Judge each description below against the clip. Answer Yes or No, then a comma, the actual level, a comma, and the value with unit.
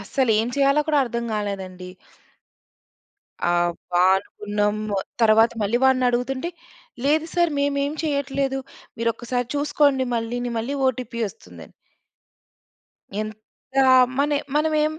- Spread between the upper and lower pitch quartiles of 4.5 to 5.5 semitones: Yes, average, 4.9 semitones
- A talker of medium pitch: No, high, 245 Hz